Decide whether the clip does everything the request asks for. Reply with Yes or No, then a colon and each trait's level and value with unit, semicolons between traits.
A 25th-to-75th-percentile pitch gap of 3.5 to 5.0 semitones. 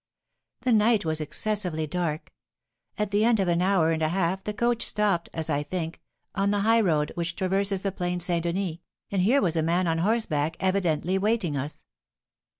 Yes: average, 3.8 semitones